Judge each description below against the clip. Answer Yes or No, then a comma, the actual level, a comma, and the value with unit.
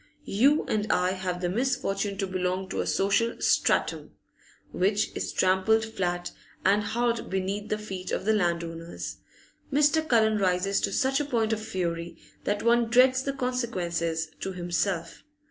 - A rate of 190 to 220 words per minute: No, average, 155 wpm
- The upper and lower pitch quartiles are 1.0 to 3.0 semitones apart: No, average, 4.3 semitones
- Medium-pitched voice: No, high, 200 Hz